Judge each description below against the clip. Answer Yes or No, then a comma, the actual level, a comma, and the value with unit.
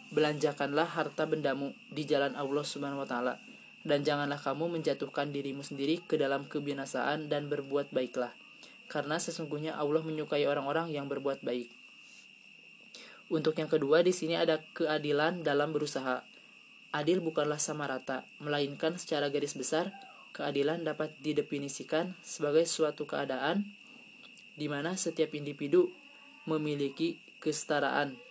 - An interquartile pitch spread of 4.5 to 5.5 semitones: No, average, 2.8 semitones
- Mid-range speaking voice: Yes, medium, 155 Hz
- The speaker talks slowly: No, average, 125 wpm